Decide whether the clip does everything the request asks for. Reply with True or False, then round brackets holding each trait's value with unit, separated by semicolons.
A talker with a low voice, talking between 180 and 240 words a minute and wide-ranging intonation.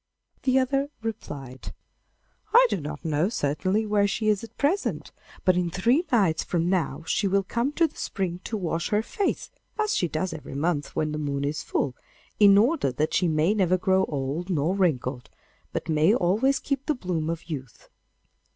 False (185 Hz; 185 wpm; 6.1 semitones)